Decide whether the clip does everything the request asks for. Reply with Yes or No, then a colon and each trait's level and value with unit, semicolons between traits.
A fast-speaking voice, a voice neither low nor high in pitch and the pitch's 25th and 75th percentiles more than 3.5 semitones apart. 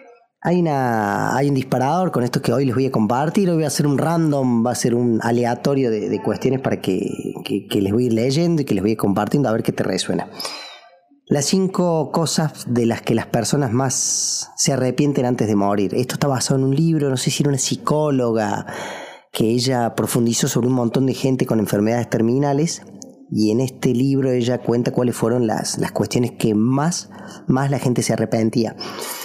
No: fast, 210 wpm; low, 130 Hz; average, 3.9 semitones